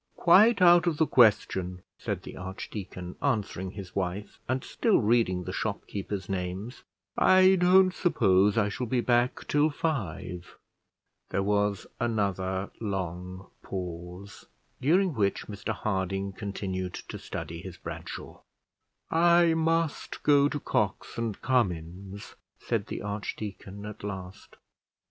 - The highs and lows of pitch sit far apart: Yes, wide, 6.4 semitones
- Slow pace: Yes, slow, 125 wpm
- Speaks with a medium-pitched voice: No, low, 100 Hz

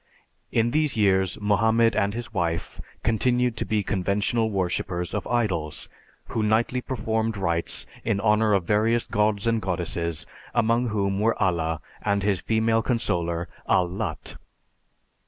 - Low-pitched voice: Yes, low, 105 Hz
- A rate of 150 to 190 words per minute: No, slow, 135 wpm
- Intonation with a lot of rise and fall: No, average, 3.3 semitones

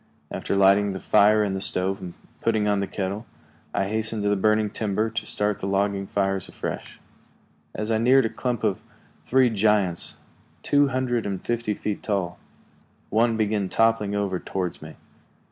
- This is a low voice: Yes, low, 105 Hz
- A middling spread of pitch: No, narrow, 2.3 semitones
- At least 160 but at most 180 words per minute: Yes, average, 170 wpm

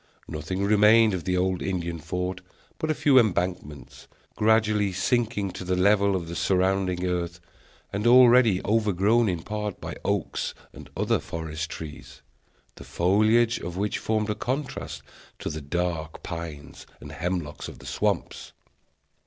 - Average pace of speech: Yes, average, 145 wpm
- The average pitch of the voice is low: Yes, very low, 95 Hz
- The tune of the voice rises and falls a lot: No, average, 3.7 semitones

